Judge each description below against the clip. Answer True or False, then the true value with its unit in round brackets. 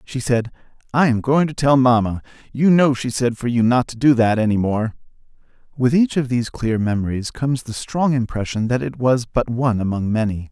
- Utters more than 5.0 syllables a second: True (5.4 syllables/s)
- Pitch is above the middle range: False (125 Hz)